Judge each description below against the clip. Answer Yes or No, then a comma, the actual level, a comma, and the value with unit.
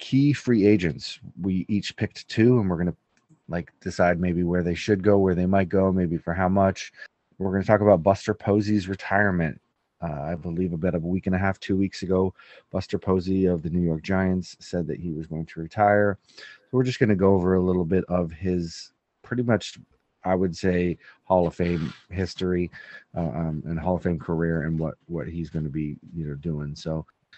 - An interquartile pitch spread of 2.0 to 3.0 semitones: Yes, narrow, 2.4 semitones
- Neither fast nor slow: No, fast, 220 wpm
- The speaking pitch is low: Yes, very low, 90 Hz